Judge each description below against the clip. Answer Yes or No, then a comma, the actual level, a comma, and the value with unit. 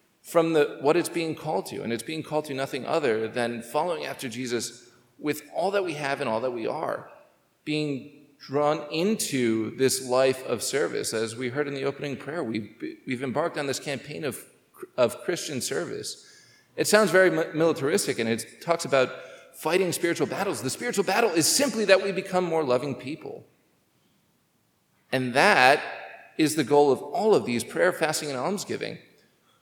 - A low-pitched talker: No, medium, 150 Hz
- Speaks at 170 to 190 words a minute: Yes, average, 175 wpm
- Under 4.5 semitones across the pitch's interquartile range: No, average, 4.8 semitones